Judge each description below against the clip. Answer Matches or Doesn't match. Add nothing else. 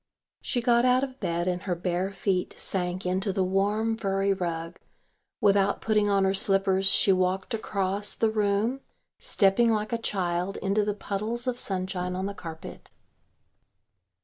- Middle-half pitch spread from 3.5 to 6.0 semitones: Doesn't match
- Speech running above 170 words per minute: Doesn't match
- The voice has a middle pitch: Doesn't match